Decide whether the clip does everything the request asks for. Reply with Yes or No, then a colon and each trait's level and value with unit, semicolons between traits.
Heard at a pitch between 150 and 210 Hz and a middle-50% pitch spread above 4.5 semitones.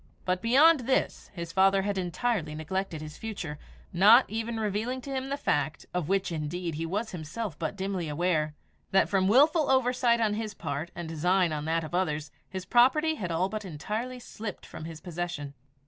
Yes: high, 190 Hz; wide, 5.6 semitones